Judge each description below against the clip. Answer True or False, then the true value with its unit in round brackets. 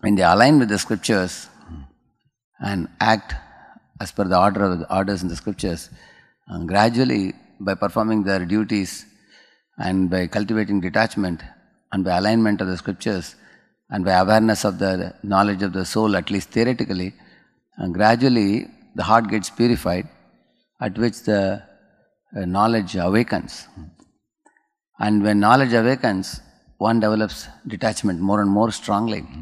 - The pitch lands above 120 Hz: False (100 Hz)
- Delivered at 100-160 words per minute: True (140 wpm)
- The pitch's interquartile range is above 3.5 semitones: False (2.8 semitones)